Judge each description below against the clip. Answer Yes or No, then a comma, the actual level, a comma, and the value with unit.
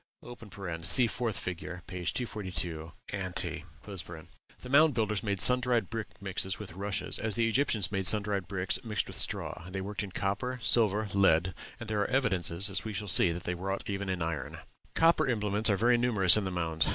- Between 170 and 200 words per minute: Yes, average, 190 wpm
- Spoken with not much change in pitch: No, average, 3.5 semitones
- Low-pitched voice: Yes, low, 100 Hz